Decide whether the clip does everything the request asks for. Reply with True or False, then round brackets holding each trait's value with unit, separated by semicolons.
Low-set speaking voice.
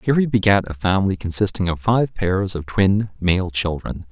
True (95 Hz)